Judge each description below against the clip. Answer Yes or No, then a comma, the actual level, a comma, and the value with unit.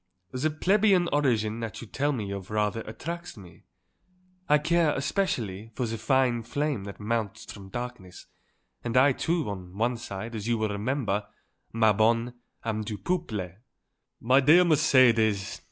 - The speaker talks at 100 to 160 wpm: Yes, average, 155 wpm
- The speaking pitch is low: Yes, low, 115 Hz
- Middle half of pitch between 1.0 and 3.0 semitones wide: No, average, 5.1 semitones